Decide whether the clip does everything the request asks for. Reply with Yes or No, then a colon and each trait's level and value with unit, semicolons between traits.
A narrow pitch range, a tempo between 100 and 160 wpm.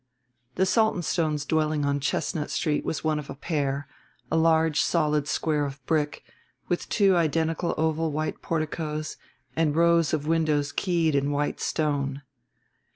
Yes: narrow, 2.0 semitones; average, 145 wpm